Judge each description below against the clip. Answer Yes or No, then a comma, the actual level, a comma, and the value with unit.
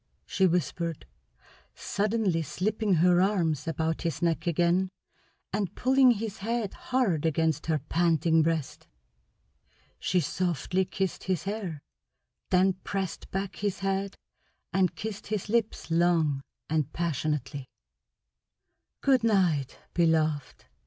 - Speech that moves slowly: Yes, slow, 110 wpm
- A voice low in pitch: No, medium, 175 Hz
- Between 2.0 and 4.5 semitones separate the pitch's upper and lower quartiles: Yes, average, 3.5 semitones